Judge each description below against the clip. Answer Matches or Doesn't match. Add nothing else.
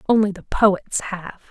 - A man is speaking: Doesn't match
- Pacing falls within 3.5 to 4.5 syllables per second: Matches